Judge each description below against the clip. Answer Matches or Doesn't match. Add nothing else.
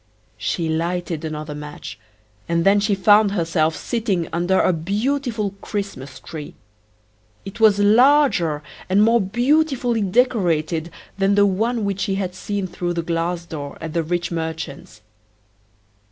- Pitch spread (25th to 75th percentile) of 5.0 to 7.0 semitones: Doesn't match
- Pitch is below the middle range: Doesn't match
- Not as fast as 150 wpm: Matches